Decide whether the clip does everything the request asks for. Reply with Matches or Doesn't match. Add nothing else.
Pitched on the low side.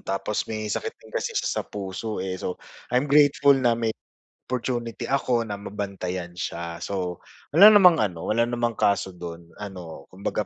Matches